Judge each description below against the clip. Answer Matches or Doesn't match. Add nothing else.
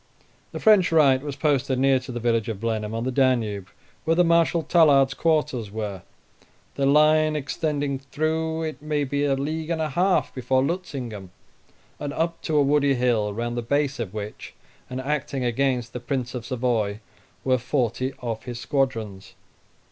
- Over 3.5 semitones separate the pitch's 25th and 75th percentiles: Matches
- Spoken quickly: Doesn't match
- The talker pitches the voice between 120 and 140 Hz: Matches